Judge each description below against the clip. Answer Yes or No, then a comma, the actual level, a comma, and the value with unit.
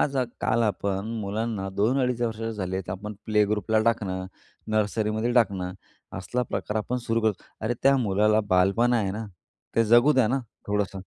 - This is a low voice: Yes, low, 110 Hz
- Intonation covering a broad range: No, average, 2.8 semitones